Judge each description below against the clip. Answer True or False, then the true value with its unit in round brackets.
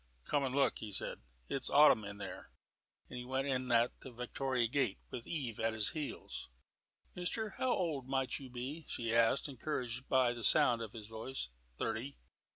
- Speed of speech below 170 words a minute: False (180 wpm)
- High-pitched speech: False (125 Hz)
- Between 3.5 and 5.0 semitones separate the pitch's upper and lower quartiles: False (3.1 semitones)